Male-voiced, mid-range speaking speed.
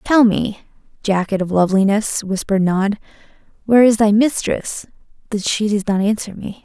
No: female; average, 155 wpm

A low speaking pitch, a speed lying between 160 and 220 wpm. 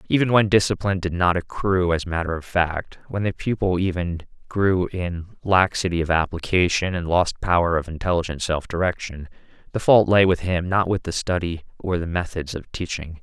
Yes: very low, 90 Hz; average, 180 wpm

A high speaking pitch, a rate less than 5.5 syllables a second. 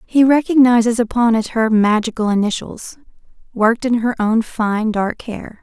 Yes: high, 230 Hz; 4.7 syllables/s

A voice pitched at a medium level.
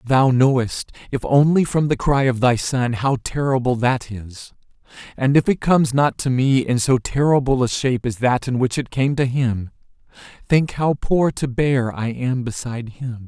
No: low, 130 Hz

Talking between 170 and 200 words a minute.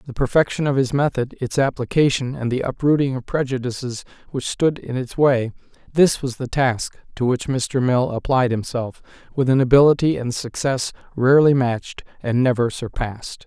No: average, 160 wpm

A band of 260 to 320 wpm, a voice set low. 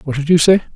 No: fast, 315 wpm; medium, 160 Hz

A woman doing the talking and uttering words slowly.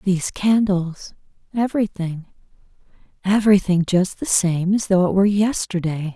Yes: female; slow, 95 wpm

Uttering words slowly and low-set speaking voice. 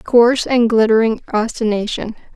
No: slow, 100 wpm; high, 225 Hz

